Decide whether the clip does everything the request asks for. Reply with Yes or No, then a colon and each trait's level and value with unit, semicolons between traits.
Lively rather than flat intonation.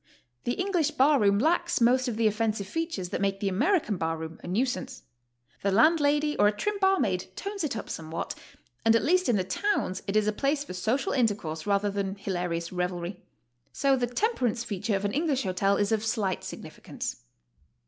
Yes: wide, 6.5 semitones